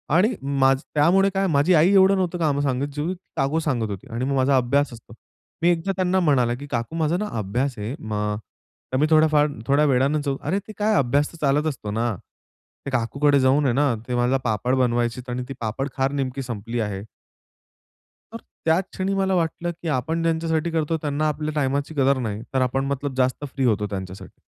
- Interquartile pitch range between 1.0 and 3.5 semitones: No, average, 4.4 semitones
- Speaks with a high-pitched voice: No, medium, 140 Hz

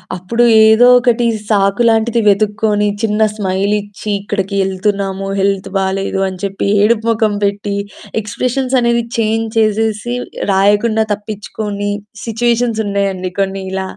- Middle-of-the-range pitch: No, high, 210 Hz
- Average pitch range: No, narrow, 2.2 semitones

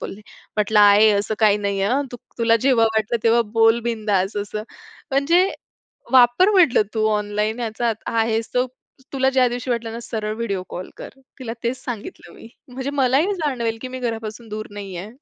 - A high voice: Yes, high, 230 Hz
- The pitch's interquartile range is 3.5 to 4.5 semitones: No, average, 2.9 semitones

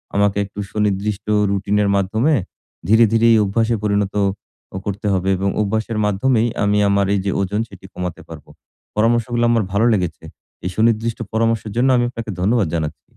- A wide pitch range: No, narrow, 2.5 semitones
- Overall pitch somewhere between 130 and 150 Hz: No, low, 105 Hz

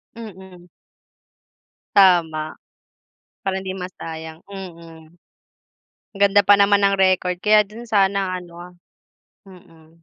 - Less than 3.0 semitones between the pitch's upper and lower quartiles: Yes, narrow, 2.6 semitones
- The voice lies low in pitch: No, medium, 185 Hz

